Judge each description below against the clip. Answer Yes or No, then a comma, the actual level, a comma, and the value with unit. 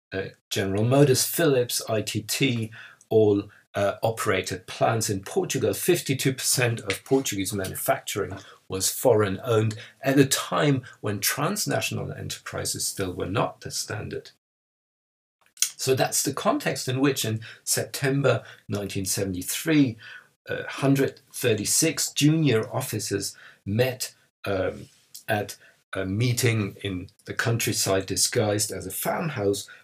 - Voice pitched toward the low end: Yes, low, 110 Hz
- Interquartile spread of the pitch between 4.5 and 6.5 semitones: Yes, average, 5.1 semitones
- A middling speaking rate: No, slow, 110 wpm